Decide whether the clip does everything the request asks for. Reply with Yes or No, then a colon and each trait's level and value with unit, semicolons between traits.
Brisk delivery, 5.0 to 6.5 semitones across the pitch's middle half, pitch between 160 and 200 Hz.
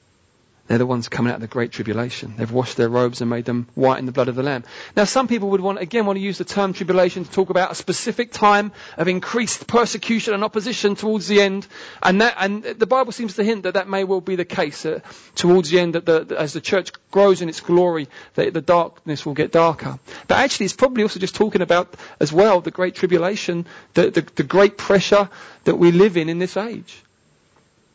No: fast, 235 wpm; average, 4.3 semitones; medium, 185 Hz